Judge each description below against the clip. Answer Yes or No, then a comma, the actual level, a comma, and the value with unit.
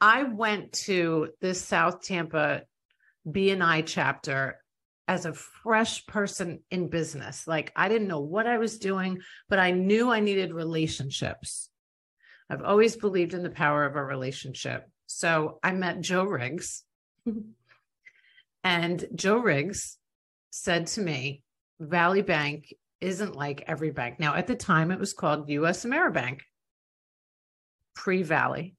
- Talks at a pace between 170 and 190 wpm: No, slow, 135 wpm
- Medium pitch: Yes, medium, 180 Hz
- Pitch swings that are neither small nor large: Yes, average, 4.3 semitones